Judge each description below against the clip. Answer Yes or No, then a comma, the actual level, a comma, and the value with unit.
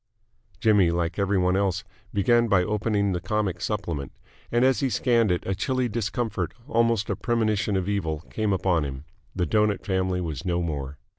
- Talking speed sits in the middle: Yes, average, 175 wpm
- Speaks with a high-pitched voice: No, low, 100 Hz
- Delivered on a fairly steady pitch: No, average, 3.5 semitones